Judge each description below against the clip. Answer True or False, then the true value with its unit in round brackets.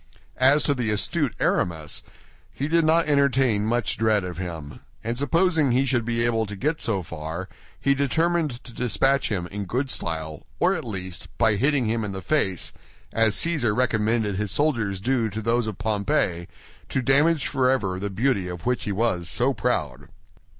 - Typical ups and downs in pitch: False (5.7 semitones)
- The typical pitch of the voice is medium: False (115 Hz)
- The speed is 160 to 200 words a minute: True (180 wpm)